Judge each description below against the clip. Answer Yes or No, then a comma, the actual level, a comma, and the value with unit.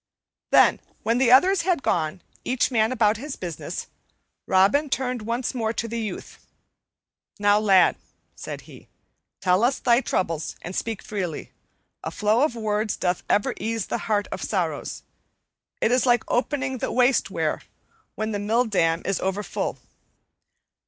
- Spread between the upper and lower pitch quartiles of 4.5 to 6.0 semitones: No, average, 3.7 semitones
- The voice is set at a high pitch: Yes, high, 220 Hz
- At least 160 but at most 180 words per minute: No, average, 150 wpm